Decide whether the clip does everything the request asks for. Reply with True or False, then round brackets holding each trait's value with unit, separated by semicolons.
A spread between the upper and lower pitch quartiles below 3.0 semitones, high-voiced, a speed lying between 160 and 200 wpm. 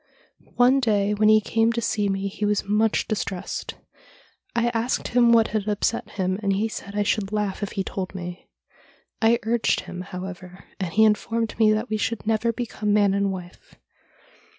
True (2.4 semitones; 210 Hz; 185 wpm)